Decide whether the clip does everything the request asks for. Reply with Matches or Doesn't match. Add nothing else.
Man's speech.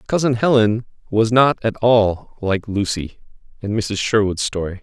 Matches